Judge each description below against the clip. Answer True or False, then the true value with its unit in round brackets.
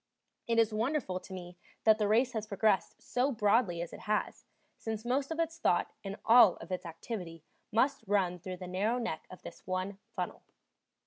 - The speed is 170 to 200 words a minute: True (190 wpm)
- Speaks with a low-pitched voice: False (210 Hz)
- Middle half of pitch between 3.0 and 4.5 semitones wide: True (4.1 semitones)